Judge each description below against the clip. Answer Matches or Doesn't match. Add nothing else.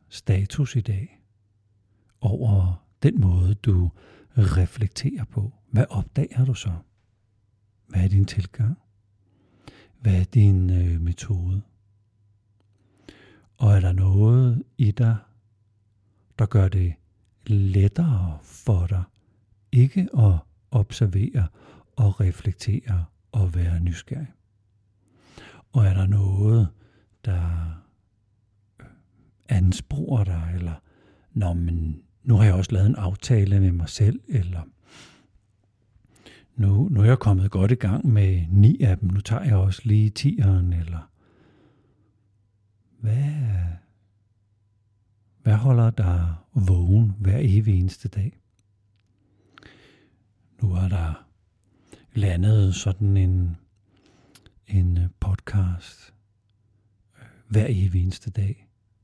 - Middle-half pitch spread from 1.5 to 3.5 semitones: Matches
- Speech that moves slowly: Matches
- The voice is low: Matches